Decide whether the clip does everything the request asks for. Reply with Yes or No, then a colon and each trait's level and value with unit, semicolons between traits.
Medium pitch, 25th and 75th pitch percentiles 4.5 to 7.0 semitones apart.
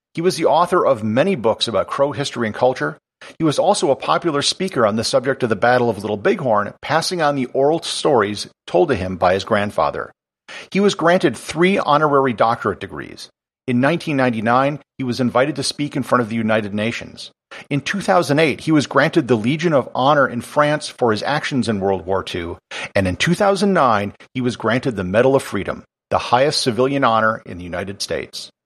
No: low, 130 Hz; average, 5.2 semitones